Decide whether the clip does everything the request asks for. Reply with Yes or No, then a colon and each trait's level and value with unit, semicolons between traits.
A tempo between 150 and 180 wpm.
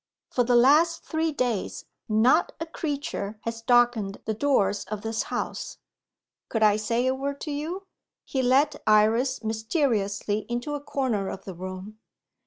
Yes: average, 155 wpm